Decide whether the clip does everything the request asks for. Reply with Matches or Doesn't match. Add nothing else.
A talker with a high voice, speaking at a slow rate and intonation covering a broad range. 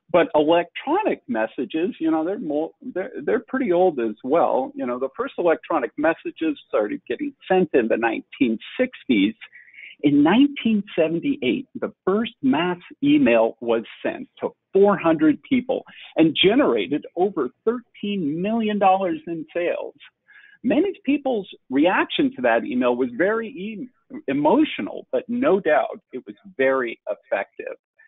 Matches